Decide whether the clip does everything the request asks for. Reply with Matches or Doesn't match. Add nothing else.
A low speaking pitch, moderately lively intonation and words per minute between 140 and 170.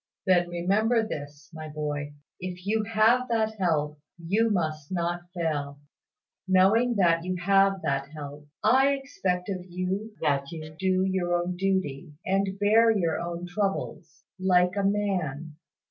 Doesn't match